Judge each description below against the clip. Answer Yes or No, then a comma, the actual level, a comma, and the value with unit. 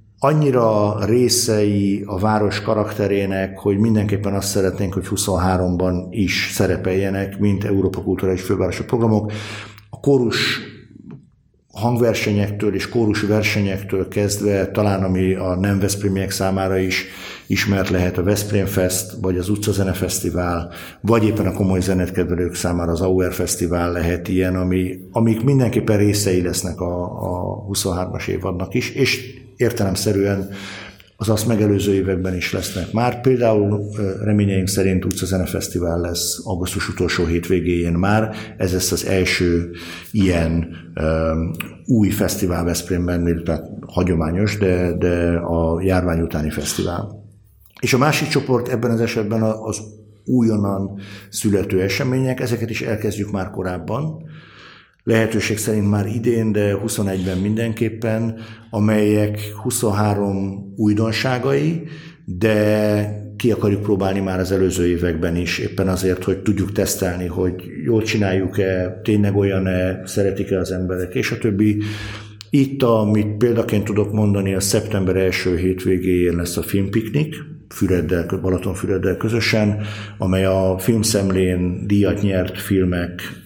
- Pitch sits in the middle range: No, low, 100 Hz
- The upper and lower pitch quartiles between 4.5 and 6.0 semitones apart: No, average, 2.7 semitones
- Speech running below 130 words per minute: Yes, average, 120 wpm